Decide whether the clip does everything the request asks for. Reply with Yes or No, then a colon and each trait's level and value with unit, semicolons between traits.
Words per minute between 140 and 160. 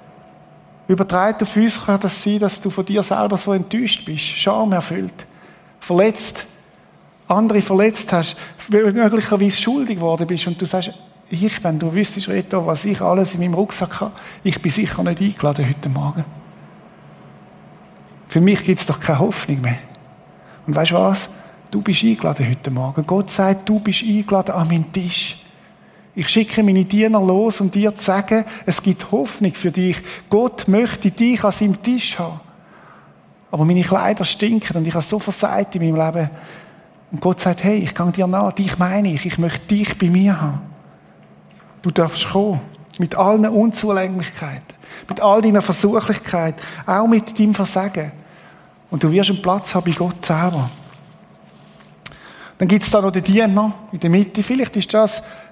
No: average, 170 wpm